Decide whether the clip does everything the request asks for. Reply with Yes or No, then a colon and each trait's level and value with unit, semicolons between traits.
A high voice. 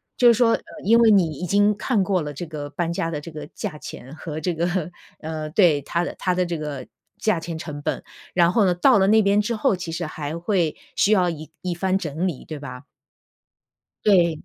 No: medium, 175 Hz